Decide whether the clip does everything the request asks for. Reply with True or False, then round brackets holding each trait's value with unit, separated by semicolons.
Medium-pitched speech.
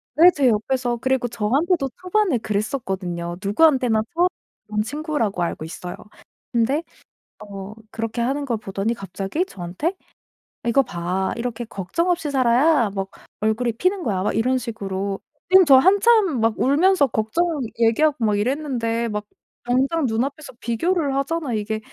False (240 Hz)